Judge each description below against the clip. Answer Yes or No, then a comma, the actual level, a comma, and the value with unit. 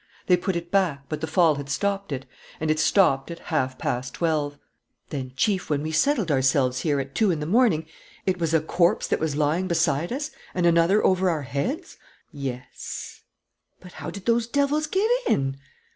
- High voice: No, medium, 165 Hz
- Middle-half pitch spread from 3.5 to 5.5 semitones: Yes, average, 5.1 semitones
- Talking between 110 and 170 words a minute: No, average, 190 wpm